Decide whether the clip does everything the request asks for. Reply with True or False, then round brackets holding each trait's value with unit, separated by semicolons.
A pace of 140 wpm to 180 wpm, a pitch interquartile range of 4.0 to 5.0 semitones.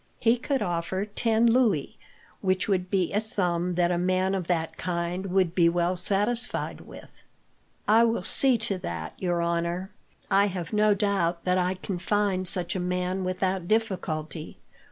False (165 wpm; 2.8 semitones)